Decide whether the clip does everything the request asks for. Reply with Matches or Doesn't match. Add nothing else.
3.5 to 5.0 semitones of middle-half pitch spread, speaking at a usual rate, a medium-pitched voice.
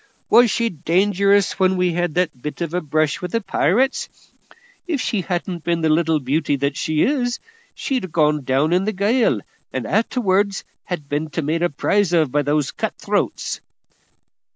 Matches